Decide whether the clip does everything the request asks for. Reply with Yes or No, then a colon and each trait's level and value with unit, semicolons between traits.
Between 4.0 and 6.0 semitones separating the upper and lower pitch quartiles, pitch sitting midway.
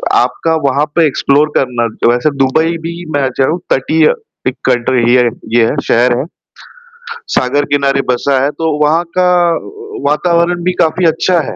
Yes: average, 4.5 semitones; medium, 145 Hz